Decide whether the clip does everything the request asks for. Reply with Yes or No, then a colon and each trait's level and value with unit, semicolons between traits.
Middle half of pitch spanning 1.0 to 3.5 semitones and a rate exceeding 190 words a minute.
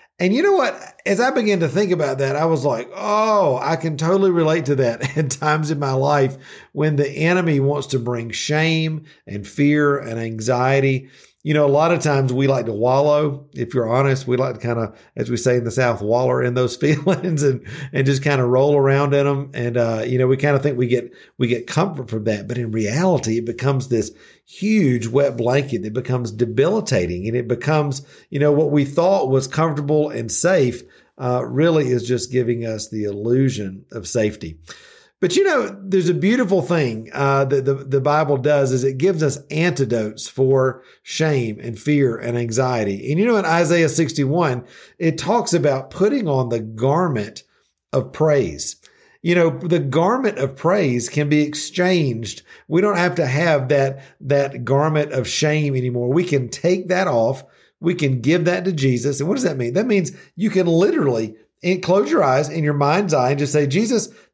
No: average, 4.7 semitones; average, 200 wpm